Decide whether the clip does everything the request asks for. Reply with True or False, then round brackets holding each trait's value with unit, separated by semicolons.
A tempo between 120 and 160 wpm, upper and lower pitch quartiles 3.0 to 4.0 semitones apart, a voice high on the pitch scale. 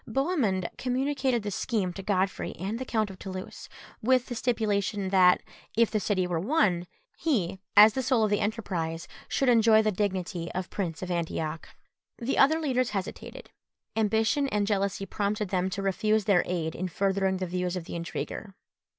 False (175 wpm; 3.6 semitones; 200 Hz)